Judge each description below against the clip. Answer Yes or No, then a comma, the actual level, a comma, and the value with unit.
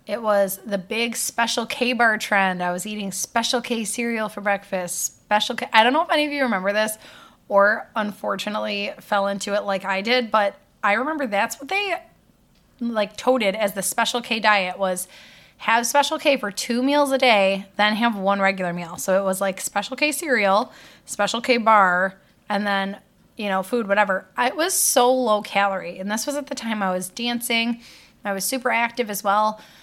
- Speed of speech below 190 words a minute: No, average, 200 wpm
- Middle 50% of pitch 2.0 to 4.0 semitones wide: Yes, average, 3.7 semitones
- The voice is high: Yes, high, 215 Hz